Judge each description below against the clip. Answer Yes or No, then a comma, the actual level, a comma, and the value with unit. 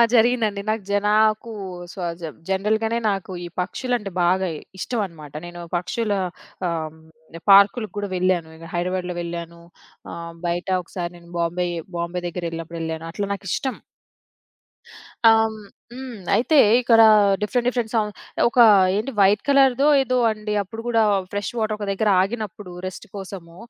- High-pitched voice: Yes, high, 195 Hz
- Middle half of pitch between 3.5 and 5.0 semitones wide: Yes, average, 4.3 semitones